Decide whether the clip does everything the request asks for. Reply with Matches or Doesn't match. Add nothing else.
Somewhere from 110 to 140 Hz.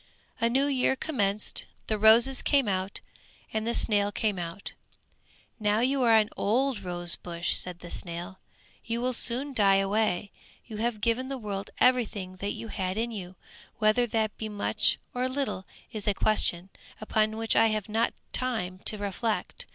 Doesn't match